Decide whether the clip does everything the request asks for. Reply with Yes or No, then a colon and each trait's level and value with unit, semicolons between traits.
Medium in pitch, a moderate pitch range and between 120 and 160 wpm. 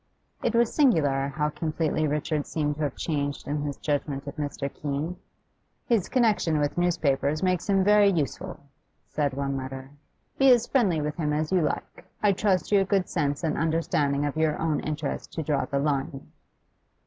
No: medium, 155 Hz; average, 4.1 semitones; average, 180 wpm